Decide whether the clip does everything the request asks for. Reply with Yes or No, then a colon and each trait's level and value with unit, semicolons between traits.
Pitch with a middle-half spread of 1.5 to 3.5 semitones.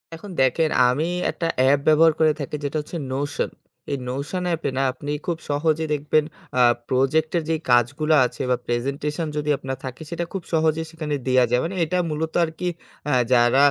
Yes: average, 3.2 semitones